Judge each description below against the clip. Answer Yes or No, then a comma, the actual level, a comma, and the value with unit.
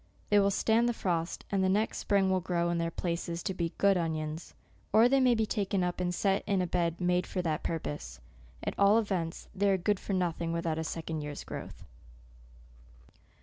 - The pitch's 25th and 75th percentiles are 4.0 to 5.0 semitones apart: No, average, 3.1 semitones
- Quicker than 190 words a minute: Yes, fast, 205 wpm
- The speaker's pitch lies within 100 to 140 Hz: No, medium, 180 Hz